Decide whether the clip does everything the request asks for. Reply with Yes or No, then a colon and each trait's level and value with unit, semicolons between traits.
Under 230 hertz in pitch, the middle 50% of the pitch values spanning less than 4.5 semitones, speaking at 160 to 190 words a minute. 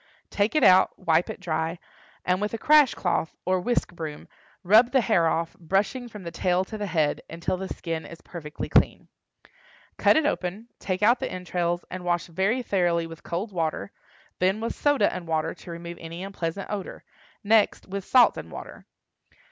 Yes: medium, 185 Hz; average, 3.8 semitones; average, 185 wpm